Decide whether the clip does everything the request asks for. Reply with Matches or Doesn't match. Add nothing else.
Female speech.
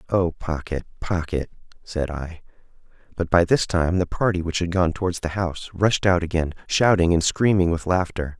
Doesn't match